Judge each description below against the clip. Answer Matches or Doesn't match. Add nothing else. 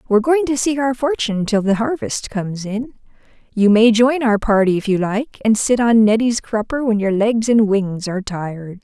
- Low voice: Doesn't match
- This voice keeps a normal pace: Doesn't match